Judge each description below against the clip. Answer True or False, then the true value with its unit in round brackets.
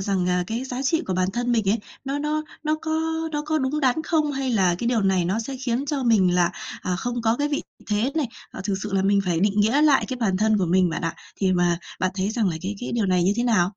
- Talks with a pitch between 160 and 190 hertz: False (220 Hz)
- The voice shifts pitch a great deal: True (6.0 semitones)